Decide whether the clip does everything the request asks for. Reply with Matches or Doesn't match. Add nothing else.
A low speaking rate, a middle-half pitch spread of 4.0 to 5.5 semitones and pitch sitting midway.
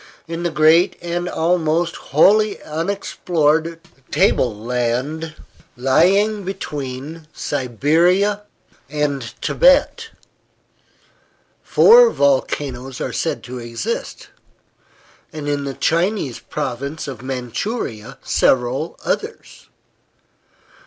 Matches